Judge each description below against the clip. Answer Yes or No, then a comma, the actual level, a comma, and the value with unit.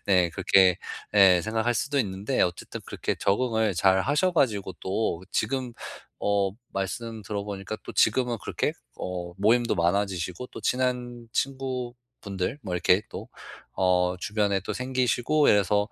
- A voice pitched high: No, low, 105 Hz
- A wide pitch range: No, average, 4.3 semitones